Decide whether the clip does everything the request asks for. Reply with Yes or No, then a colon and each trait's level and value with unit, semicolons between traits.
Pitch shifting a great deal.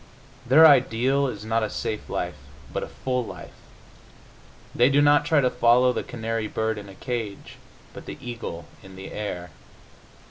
No: average, 3.4 semitones